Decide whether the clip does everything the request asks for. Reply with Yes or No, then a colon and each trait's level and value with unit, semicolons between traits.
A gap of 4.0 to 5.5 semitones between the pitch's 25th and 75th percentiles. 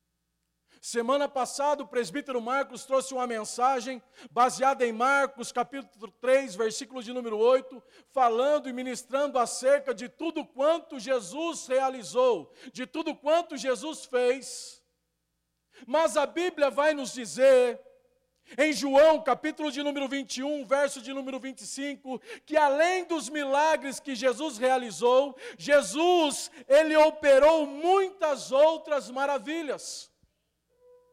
No: average, 3.2 semitones